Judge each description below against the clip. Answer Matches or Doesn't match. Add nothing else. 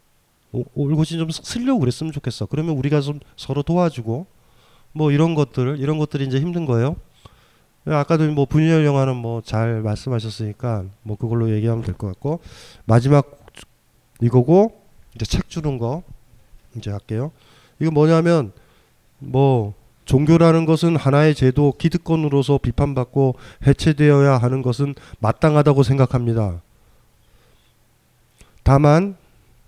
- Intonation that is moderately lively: Matches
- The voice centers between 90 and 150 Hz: Matches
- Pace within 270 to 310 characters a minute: Matches